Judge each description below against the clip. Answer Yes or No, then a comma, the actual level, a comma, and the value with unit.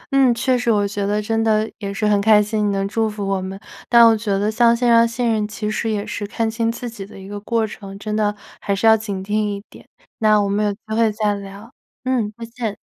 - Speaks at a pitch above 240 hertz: No, high, 215 Hz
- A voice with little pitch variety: Yes, narrow, 1.9 semitones